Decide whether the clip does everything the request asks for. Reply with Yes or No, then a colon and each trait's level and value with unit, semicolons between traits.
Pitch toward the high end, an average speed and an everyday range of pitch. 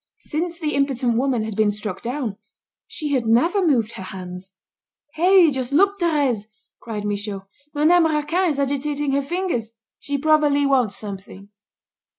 No: very high, 275 Hz; average, 150 wpm; wide, 6.0 semitones